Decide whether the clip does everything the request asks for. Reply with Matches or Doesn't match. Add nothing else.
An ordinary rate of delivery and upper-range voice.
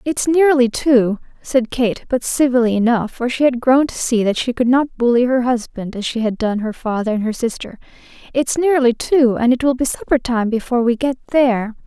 Doesn't match